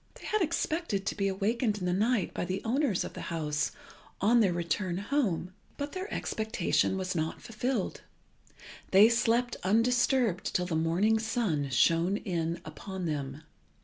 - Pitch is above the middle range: Yes, high, 195 Hz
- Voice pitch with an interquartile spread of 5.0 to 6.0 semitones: Yes, average, 5.3 semitones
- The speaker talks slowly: No, average, 155 wpm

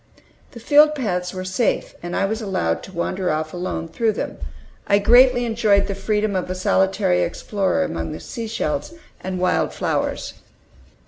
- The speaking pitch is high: Yes, high, 195 Hz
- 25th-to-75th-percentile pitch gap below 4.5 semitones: Yes, average, 3.8 semitones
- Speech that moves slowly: No, average, 165 wpm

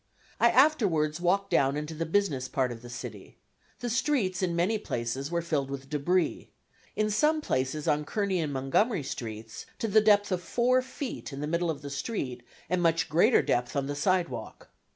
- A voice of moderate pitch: Yes, medium, 165 Hz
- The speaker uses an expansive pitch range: Yes, wide, 6.8 semitones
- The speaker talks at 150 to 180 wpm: No, average, 190 wpm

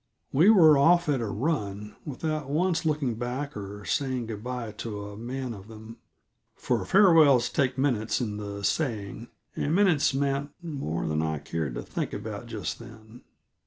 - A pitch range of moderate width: No, wide, 5.8 semitones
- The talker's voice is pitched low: Yes, low, 125 Hz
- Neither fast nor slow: Yes, average, 165 wpm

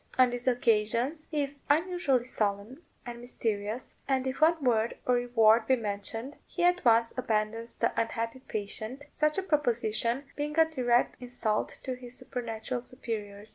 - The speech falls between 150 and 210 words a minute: Yes, average, 155 wpm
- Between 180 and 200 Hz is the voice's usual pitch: No, high, 245 Hz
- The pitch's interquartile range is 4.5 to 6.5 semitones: No, average, 3.4 semitones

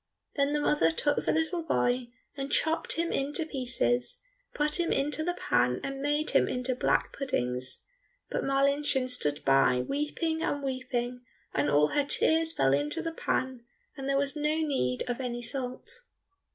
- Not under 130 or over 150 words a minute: No, average, 165 wpm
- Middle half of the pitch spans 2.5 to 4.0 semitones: Yes, average, 3.7 semitones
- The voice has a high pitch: Yes, very high, 275 Hz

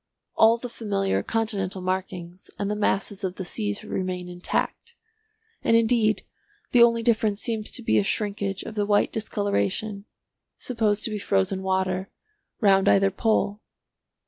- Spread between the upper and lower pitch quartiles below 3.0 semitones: Yes, narrow, 2.5 semitones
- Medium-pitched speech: No, high, 205 Hz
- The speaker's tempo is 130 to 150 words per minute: Yes, average, 145 wpm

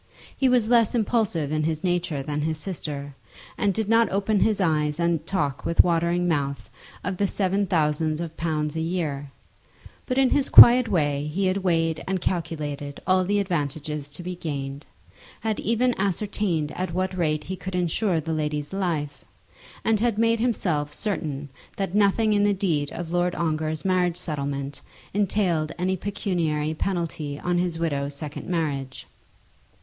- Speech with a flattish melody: No, average, 4.4 semitones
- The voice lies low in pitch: No, medium, 170 Hz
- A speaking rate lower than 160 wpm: No, average, 165 wpm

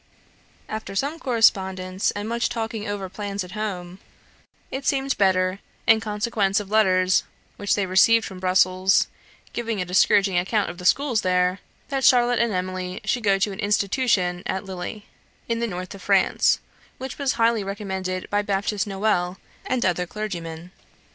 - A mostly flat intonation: No, average, 3.3 semitones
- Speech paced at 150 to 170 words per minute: Yes, average, 160 wpm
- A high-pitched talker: Yes, high, 200 Hz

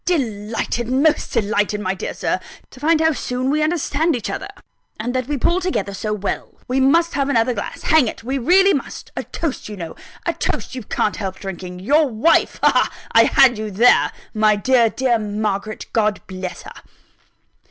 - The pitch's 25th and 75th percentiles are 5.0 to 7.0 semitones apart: Yes, average, 5.3 semitones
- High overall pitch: Yes, high, 240 Hz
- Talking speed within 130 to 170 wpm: No, average, 190 wpm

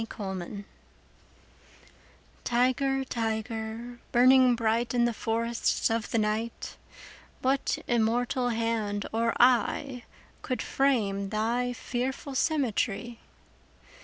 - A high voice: Yes, high, 235 Hz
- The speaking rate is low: Yes, slow, 95 wpm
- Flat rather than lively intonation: Yes, narrow, 2.1 semitones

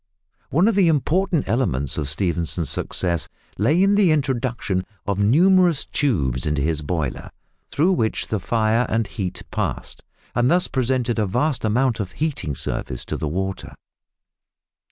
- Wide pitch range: Yes, wide, 8.9 semitones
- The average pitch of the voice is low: Yes, low, 115 Hz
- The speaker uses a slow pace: No, average, 150 wpm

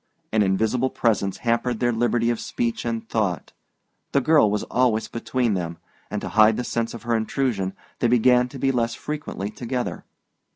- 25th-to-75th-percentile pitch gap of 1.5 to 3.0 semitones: Yes, narrow, 2.5 semitones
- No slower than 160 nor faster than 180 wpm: Yes, average, 175 wpm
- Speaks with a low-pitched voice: Yes, low, 115 Hz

